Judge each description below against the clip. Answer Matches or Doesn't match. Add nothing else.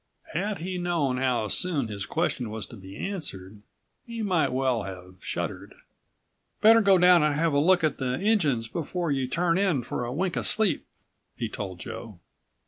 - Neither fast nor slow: Matches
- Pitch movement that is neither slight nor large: Doesn't match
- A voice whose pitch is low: Doesn't match